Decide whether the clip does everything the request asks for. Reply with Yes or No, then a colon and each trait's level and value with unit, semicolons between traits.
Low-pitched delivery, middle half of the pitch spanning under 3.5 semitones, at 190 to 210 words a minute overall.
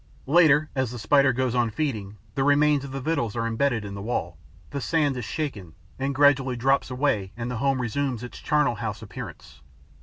No: low, 130 Hz; average, 3.8 semitones; average, 195 wpm